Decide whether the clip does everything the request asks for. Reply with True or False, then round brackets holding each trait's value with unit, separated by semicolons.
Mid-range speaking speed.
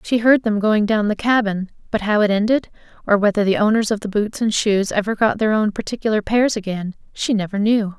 False (225 wpm)